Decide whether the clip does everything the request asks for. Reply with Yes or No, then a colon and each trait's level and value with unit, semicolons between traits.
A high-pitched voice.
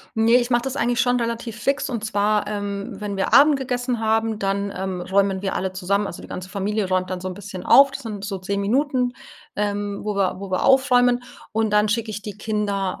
Yes: high, 210 Hz